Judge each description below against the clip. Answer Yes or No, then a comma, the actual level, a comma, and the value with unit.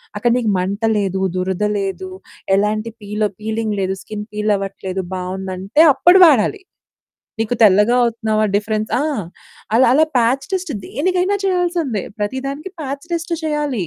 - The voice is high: Yes, high, 215 Hz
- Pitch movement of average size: No, wide, 6.1 semitones